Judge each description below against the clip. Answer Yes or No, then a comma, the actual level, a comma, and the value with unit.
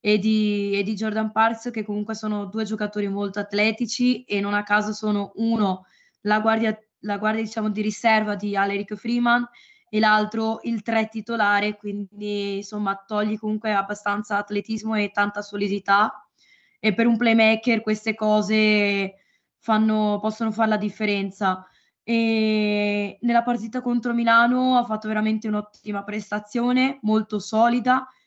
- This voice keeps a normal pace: Yes, average, 140 wpm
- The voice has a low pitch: No, high, 215 Hz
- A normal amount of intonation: No, narrow, 1.4 semitones